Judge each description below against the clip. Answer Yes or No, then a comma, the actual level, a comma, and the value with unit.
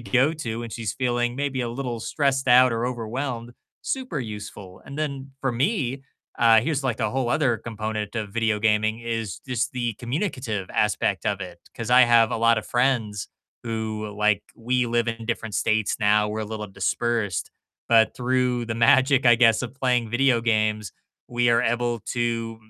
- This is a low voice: Yes, low, 115 Hz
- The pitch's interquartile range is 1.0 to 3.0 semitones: Yes, narrow, 2.5 semitones